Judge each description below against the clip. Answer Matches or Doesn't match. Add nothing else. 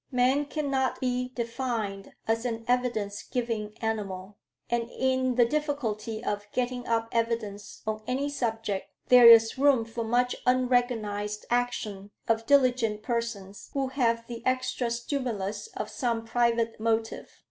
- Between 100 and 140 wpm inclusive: Matches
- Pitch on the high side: Matches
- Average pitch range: Doesn't match